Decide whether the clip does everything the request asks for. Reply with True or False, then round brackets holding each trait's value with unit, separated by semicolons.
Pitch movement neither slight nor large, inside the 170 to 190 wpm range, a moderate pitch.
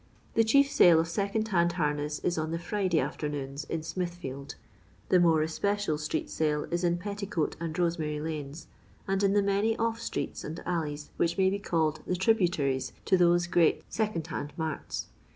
True (4.2 semitones; 180 wpm; 170 Hz)